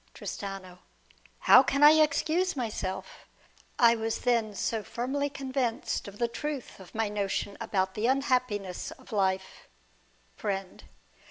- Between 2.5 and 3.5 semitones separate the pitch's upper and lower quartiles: No, average, 5.1 semitones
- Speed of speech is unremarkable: No, slow, 125 wpm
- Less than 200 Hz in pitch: No, high, 225 Hz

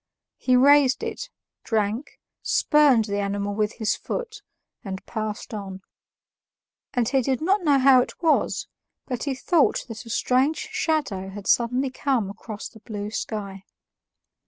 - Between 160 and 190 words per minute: No, average, 145 wpm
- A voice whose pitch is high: Yes, high, 240 Hz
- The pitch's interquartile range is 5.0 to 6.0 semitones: Yes, average, 5.3 semitones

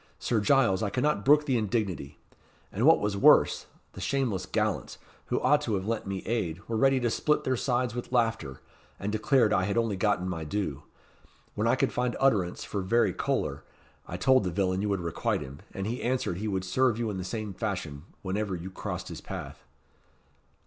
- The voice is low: Yes, low, 105 Hz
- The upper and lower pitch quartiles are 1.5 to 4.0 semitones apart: No, average, 4.4 semitones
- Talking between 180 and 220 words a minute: Yes, average, 200 wpm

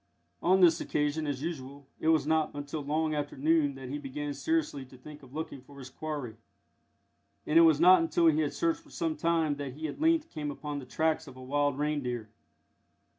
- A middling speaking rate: No, fast, 210 wpm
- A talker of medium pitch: Yes, medium, 150 Hz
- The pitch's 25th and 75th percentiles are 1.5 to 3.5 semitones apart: Yes, narrow, 2.4 semitones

